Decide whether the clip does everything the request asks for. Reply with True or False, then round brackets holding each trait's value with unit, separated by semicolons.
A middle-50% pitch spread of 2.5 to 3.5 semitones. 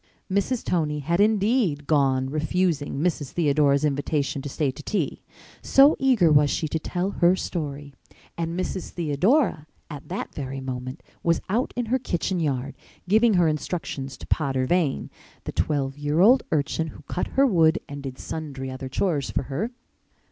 False (4.6 semitones)